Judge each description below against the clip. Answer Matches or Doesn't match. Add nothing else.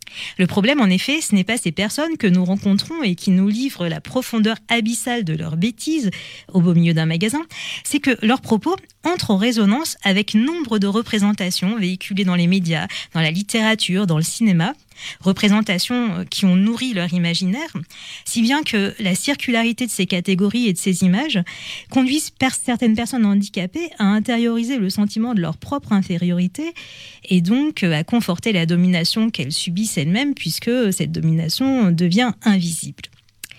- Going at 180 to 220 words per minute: Doesn't match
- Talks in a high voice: Matches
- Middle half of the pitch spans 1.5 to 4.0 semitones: Doesn't match